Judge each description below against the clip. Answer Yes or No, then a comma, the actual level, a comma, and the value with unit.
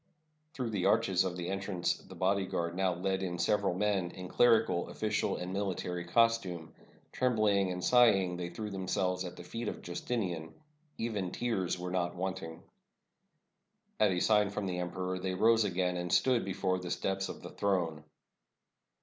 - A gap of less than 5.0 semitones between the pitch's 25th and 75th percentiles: Yes, narrow, 2.5 semitones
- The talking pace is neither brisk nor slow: Yes, average, 165 wpm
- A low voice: Yes, very low, 95 Hz